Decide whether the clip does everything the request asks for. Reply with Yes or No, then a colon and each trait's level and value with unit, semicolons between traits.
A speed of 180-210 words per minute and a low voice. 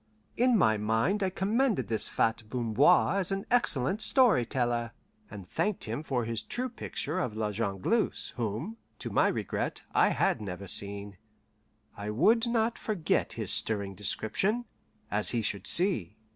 No: average, 155 wpm; low, 125 Hz